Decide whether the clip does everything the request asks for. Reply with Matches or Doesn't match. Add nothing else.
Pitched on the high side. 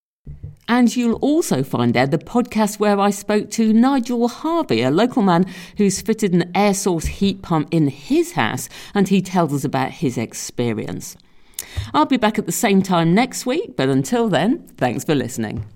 Matches